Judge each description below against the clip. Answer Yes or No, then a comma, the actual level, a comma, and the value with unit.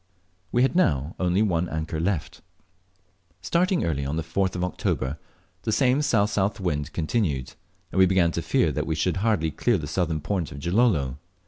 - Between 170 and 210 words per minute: Yes, average, 180 wpm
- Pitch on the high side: No, very low, 90 Hz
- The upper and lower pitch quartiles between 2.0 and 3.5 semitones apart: No, average, 4.8 semitones